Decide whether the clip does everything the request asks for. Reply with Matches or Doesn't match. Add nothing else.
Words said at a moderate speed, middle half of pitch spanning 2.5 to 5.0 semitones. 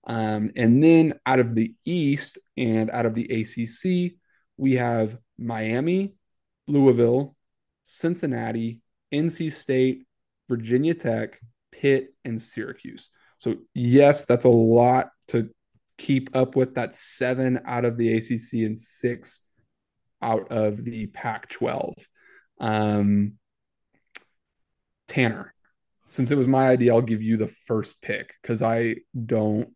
Doesn't match